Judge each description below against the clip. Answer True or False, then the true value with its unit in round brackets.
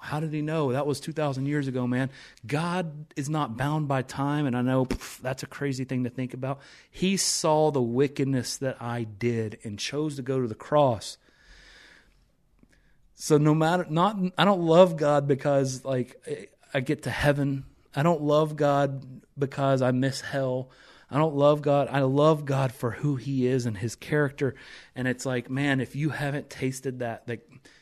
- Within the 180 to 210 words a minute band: True (190 wpm)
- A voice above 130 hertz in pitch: True (140 Hz)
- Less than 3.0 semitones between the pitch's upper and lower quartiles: True (2.4 semitones)